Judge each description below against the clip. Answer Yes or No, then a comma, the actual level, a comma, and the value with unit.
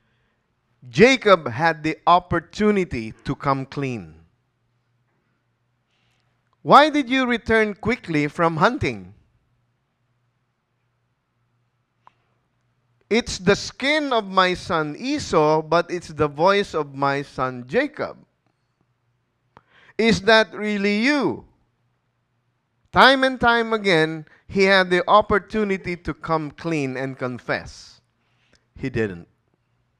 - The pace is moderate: No, slow, 95 wpm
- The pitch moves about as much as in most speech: No, wide, 8.8 semitones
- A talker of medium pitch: Yes, medium, 155 Hz